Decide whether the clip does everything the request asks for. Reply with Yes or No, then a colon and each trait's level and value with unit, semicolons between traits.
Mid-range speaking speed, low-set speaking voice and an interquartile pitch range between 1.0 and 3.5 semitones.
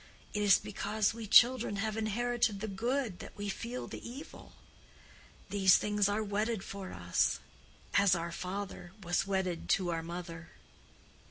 No: average, 150 wpm; high, 200 Hz; average, 3.1 semitones